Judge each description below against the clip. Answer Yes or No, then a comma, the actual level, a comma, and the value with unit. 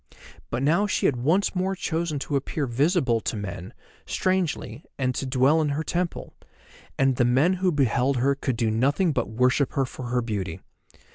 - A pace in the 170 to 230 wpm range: Yes, average, 185 wpm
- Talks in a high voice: No, low, 135 Hz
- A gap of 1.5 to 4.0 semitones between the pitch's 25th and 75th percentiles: No, average, 4.8 semitones